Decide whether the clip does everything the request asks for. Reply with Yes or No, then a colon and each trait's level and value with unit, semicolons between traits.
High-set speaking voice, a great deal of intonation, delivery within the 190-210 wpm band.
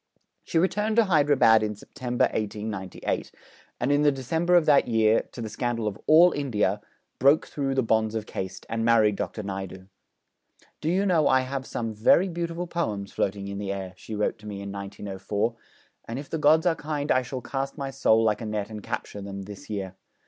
No: low, 115 Hz; wide, 5.9 semitones; average, 200 wpm